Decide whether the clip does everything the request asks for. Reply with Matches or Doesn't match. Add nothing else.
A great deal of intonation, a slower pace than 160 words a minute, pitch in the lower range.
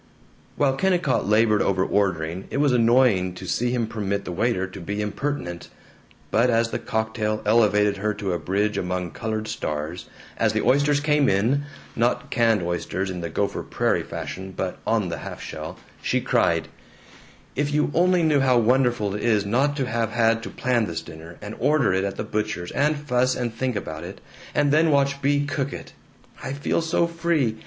Doesn't match